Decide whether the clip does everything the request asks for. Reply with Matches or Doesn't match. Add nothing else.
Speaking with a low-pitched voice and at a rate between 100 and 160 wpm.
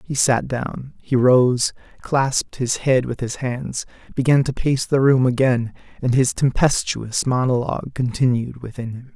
Matches